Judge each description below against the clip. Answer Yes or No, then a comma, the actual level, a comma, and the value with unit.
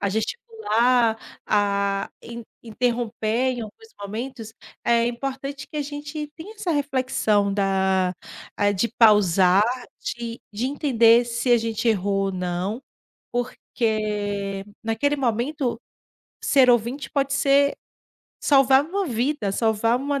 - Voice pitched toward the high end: Yes, high, 235 Hz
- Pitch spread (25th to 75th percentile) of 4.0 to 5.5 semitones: Yes, average, 4.7 semitones